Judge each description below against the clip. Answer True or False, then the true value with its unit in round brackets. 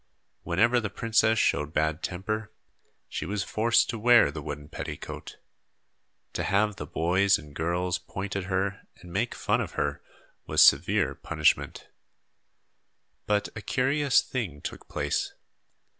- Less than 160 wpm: True (140 wpm)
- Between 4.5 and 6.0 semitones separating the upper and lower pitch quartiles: True (4.8 semitones)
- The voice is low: True (95 Hz)